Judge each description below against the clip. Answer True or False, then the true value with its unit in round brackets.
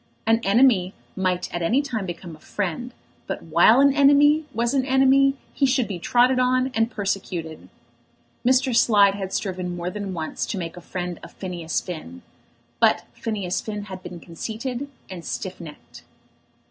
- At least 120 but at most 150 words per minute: False (165 wpm)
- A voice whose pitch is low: False (205 Hz)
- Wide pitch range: True (6.0 semitones)